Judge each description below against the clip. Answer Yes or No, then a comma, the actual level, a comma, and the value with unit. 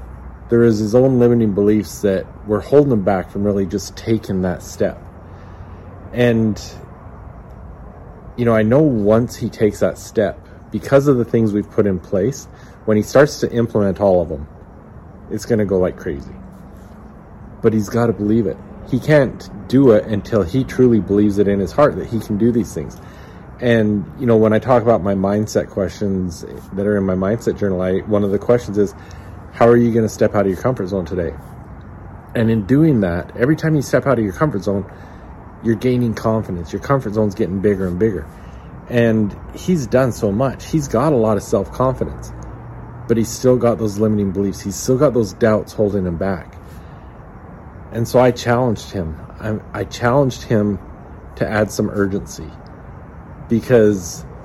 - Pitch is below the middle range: Yes, low, 105 Hz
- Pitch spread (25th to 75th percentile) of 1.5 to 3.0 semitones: No, average, 3.4 semitones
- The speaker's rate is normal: Yes, average, 185 wpm